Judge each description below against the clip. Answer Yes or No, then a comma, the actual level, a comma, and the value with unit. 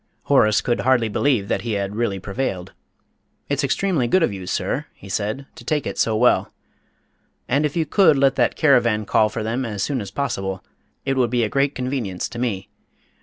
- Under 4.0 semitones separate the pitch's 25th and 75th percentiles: No, average, 4.9 semitones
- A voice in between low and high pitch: No, low, 120 Hz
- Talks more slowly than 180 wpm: No, fast, 205 wpm